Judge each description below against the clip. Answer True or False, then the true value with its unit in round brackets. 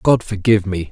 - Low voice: True (100 Hz)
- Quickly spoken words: False (195 wpm)